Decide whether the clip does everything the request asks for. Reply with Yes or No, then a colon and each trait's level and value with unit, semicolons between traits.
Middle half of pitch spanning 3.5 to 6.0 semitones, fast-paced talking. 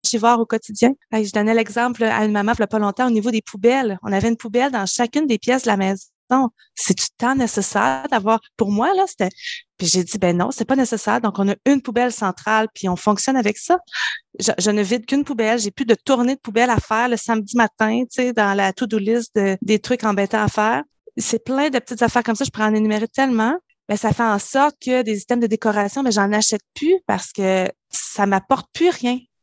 No: average, 3.1 semitones; fast, 245 wpm